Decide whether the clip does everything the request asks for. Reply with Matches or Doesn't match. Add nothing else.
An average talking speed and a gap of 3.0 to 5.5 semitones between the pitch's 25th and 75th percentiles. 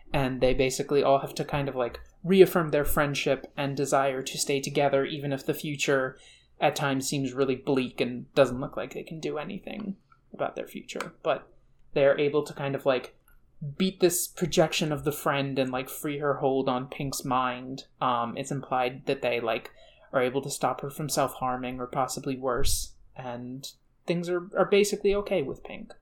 Doesn't match